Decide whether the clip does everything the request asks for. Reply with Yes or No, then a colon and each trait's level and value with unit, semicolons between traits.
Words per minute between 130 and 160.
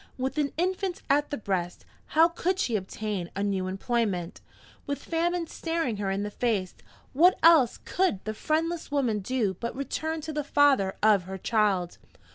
No: average, 170 wpm